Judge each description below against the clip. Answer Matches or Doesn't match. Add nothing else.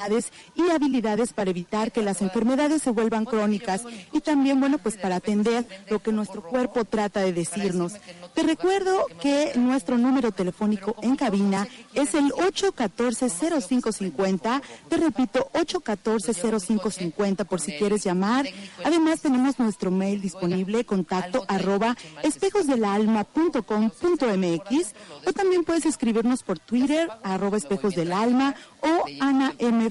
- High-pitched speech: Matches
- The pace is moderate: Doesn't match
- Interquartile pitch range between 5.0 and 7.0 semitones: Matches